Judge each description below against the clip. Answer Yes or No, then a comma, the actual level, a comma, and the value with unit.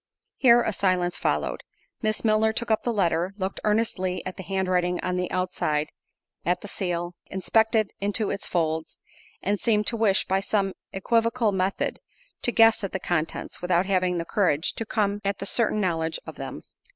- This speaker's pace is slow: No, average, 165 wpm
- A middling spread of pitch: Yes, average, 3.2 semitones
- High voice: Yes, high, 195 Hz